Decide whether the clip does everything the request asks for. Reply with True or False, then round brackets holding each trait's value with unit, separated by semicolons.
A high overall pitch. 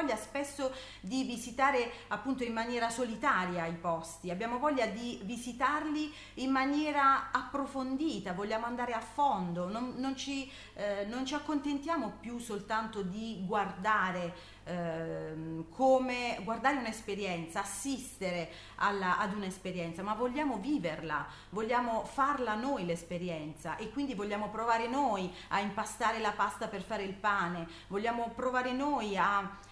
True (225 Hz)